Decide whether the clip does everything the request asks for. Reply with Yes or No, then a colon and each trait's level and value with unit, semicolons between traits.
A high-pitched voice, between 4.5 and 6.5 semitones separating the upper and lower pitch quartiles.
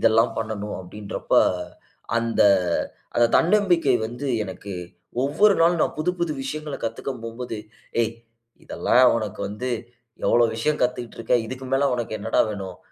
No: low, 120 Hz; average, 4.8 semitones